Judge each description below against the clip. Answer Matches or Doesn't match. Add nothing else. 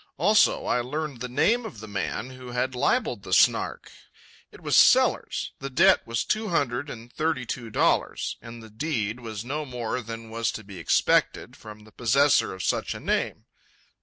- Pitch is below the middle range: Matches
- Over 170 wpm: Matches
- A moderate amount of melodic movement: Matches